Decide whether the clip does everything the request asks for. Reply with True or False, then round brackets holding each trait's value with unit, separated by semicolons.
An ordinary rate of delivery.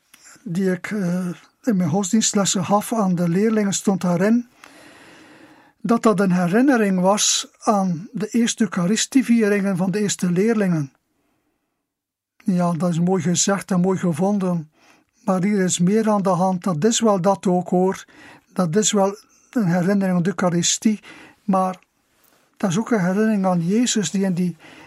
True (155 wpm)